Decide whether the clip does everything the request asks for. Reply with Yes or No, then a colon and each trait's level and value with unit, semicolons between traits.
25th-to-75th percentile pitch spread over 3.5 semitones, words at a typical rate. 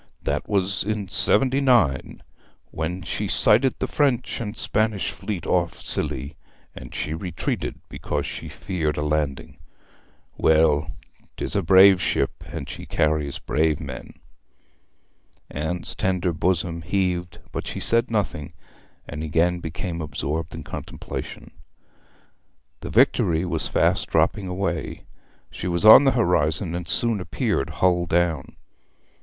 No: average, 4.1 semitones; slow, 130 wpm